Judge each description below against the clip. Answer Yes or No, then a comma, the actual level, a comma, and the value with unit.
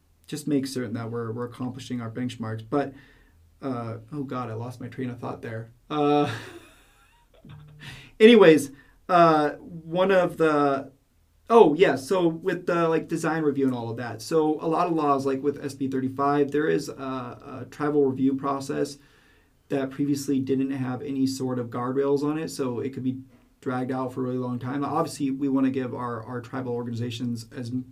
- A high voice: No, low, 135 Hz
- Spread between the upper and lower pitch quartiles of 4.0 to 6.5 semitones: No, average, 2.7 semitones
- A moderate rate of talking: Yes, average, 180 wpm